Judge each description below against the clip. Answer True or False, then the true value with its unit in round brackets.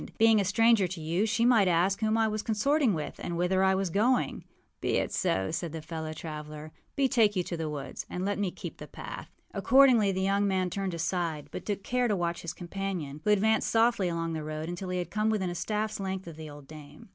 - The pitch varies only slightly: False (4.4 semitones)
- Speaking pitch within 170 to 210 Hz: True (190 Hz)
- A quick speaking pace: True (235 wpm)